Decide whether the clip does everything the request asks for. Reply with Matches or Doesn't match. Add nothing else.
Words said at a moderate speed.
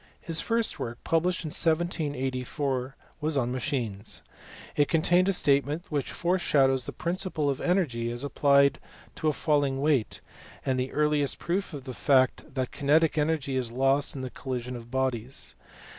Matches